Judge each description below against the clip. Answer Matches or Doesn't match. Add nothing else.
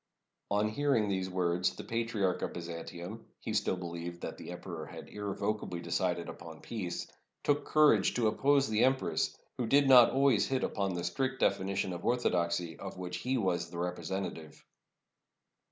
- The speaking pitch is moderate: Doesn't match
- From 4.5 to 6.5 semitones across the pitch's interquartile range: Matches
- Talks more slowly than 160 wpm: Doesn't match